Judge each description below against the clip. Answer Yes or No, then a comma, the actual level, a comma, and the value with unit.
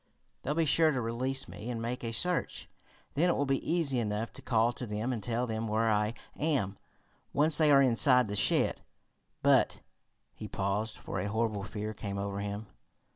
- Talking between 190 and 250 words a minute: Yes, average, 195 wpm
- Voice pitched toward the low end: Yes, low, 115 Hz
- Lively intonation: No, average, 4.2 semitones